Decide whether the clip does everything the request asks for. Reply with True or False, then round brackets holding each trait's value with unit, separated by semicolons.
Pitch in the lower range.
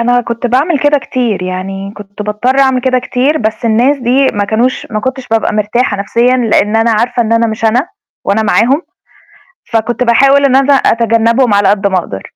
False (235 Hz)